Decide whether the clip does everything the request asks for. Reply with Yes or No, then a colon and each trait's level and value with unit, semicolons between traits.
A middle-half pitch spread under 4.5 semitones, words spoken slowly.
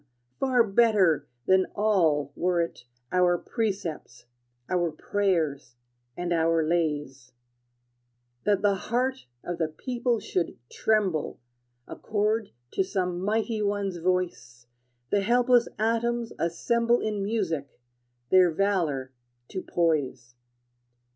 No: average, 4.9 semitones; slow, 105 wpm